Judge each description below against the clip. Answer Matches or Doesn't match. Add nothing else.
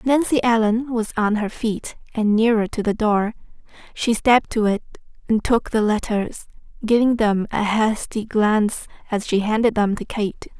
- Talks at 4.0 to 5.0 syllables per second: Matches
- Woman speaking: Matches